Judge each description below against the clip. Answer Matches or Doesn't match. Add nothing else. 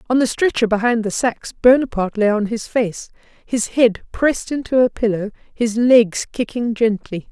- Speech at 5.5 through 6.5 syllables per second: Doesn't match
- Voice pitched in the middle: Doesn't match